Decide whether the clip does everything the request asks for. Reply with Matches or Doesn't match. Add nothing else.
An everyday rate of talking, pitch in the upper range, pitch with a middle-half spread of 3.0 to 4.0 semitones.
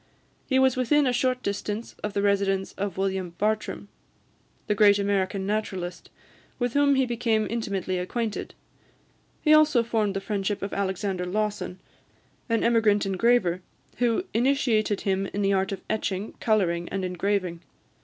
Matches